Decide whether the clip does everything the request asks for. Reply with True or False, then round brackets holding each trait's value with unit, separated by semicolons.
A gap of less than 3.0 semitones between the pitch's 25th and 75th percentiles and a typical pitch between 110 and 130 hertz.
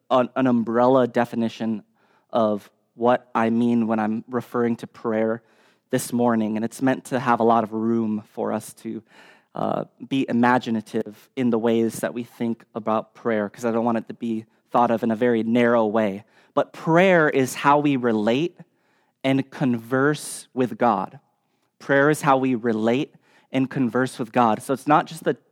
True (2.6 semitones; 120 Hz)